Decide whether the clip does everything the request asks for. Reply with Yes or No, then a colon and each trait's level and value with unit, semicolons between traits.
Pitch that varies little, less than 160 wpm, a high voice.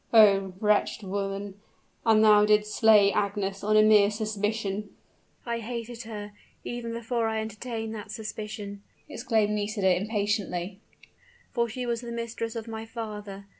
Yes: narrow, 1.8 semitones; average, 140 wpm; high, 215 Hz